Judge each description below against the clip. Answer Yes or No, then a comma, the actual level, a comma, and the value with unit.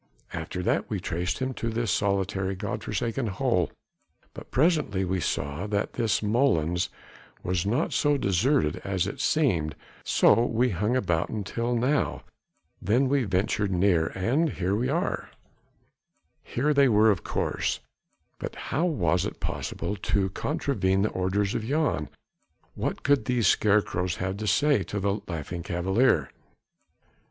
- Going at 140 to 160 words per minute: Yes, average, 145 wpm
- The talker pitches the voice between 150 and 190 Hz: No, low, 100 Hz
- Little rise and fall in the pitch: No, average, 5.2 semitones